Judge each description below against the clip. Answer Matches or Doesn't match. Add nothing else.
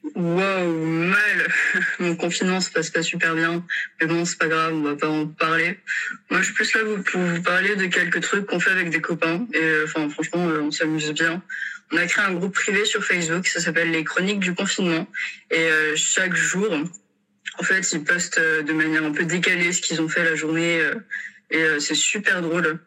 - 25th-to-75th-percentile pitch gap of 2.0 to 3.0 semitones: Matches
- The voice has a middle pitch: Matches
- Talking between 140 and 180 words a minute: Doesn't match